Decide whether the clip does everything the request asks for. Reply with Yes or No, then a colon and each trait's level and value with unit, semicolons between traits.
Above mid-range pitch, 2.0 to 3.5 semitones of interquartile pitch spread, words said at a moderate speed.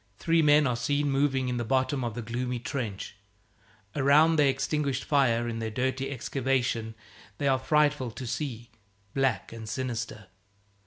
No: low, 130 Hz; average, 3.0 semitones; average, 155 wpm